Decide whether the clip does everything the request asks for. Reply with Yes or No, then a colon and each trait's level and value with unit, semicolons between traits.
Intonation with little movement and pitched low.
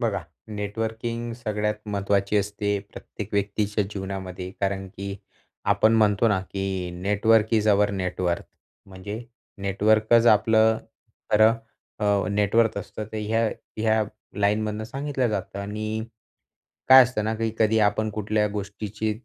Yes: narrow, 1.8 semitones; low, 105 Hz